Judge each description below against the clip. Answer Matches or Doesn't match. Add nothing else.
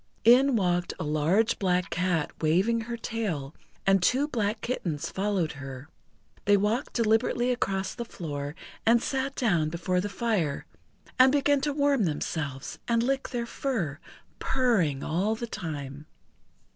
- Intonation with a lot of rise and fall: Matches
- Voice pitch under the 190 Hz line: Doesn't match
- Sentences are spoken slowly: Doesn't match